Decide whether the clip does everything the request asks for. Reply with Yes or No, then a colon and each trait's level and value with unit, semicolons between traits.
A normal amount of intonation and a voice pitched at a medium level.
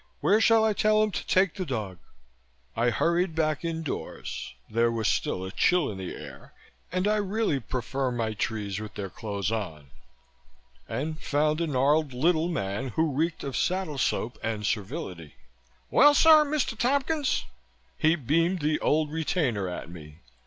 No: wide, 8.6 semitones; medium, 150 Hz